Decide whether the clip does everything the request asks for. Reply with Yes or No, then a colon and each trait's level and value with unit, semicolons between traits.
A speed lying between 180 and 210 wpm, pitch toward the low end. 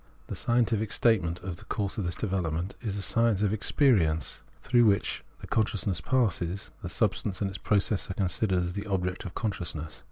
Yes: average, 185 wpm; low, 100 Hz